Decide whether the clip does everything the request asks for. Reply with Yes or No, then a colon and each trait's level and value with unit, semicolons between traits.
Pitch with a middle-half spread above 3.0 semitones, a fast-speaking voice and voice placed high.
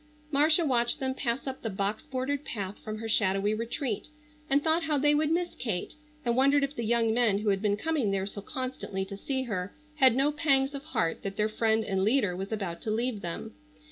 Yes: average, 5.2 semitones; fast, 220 wpm; high, 235 Hz